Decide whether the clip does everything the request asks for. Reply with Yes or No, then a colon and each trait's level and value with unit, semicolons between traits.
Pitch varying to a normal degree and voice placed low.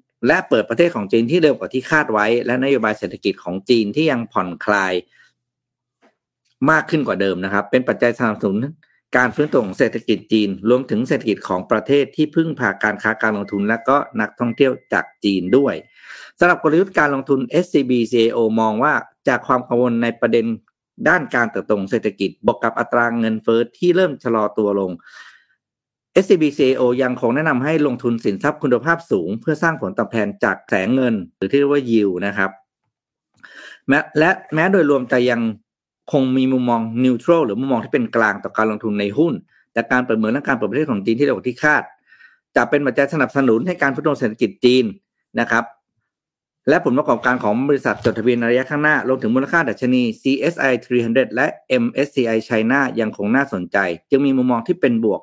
Yes: average, 4.2 semitones; low, 125 Hz